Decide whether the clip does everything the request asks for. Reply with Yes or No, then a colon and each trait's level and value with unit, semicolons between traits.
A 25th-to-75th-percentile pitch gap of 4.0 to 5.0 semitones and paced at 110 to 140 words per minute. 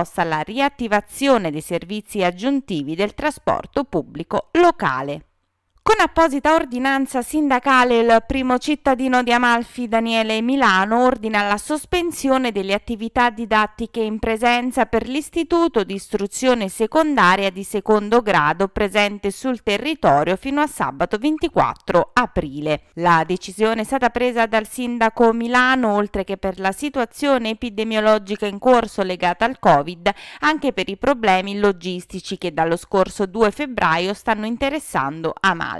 Yes: average, 4.7 semitones; average, 125 wpm